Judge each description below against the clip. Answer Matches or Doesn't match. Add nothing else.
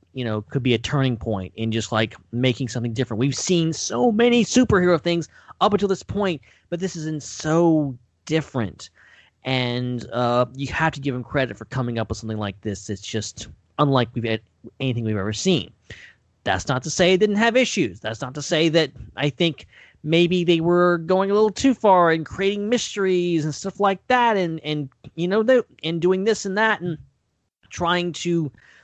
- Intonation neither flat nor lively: Doesn't match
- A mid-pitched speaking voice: Matches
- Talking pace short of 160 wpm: Doesn't match